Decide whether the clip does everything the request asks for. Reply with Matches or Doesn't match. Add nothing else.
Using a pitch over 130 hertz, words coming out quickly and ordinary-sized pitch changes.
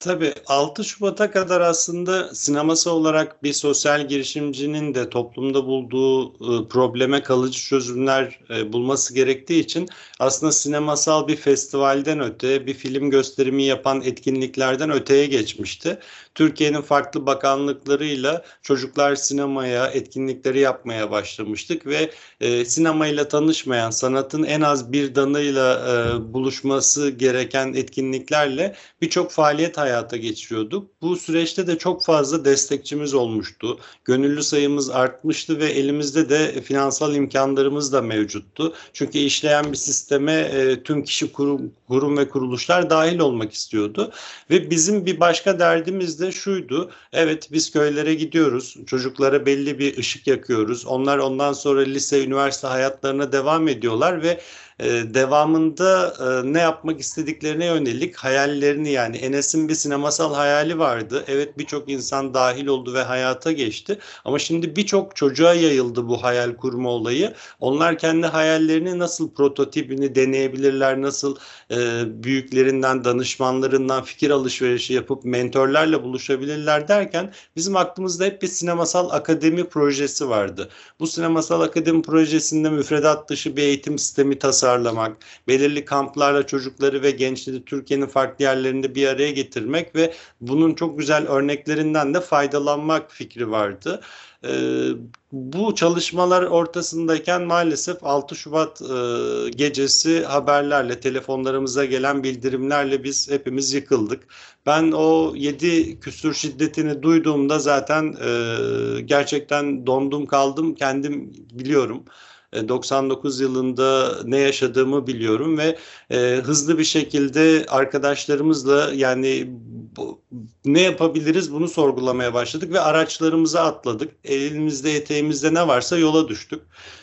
Doesn't match